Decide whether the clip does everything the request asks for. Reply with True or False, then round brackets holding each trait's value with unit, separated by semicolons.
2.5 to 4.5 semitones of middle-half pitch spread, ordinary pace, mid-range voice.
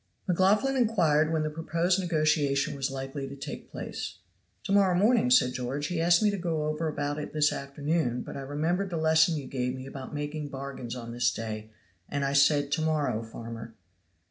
True (3.6 semitones; 195 wpm; 145 Hz)